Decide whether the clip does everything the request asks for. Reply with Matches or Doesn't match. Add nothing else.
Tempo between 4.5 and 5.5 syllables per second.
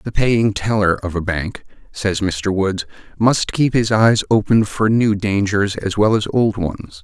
Doesn't match